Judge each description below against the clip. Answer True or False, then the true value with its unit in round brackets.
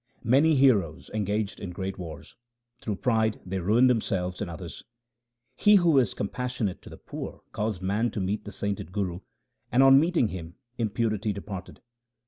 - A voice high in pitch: False (105 Hz)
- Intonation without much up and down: False (4.3 semitones)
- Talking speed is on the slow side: False (160 wpm)